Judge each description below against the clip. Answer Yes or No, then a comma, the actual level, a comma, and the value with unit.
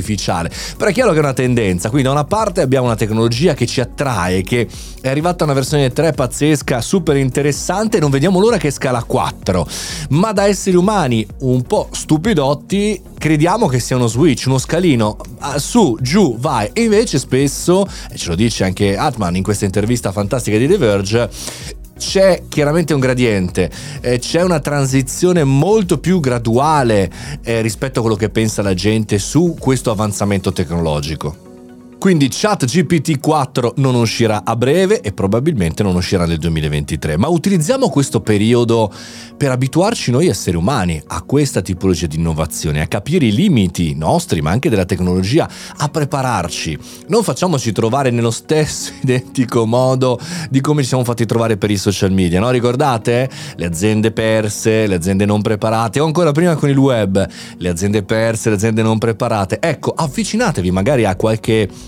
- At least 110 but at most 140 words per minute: No, average, 165 wpm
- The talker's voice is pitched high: No, low, 125 Hz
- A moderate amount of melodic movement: No, wide, 6.0 semitones